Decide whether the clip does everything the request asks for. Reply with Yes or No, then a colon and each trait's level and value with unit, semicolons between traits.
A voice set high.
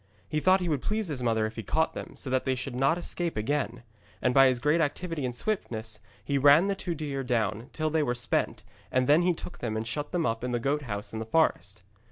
No: low, 135 Hz